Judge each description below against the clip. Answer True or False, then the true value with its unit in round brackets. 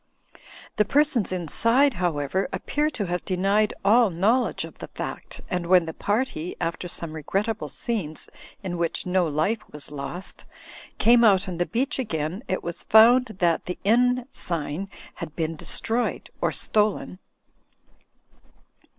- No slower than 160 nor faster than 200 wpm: False (150 wpm)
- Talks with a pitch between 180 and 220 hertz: True (190 Hz)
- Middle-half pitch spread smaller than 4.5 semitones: False (5.1 semitones)